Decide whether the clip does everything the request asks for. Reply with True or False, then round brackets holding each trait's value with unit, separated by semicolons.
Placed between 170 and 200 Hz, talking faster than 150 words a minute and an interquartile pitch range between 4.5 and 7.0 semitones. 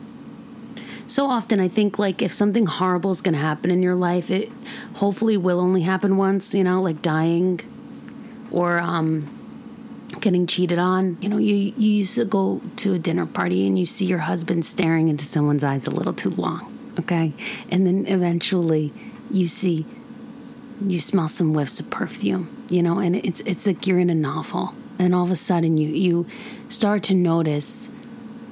True (190 Hz; 180 wpm; 4.9 semitones)